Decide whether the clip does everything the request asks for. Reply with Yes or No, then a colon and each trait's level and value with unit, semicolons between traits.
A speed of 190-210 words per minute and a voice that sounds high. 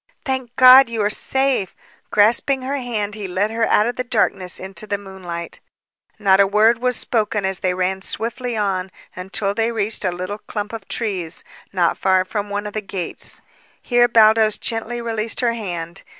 No: average, 180 wpm; high, 210 Hz